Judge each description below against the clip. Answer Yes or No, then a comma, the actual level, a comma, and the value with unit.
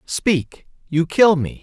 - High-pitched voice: No, medium, 170 Hz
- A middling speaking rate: Yes, average, 145 wpm